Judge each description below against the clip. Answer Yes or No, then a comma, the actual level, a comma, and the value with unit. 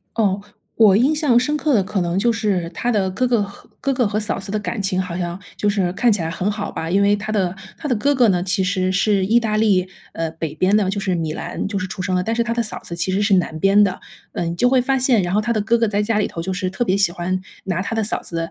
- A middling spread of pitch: Yes, average, 3.4 semitones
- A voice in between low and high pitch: No, high, 200 Hz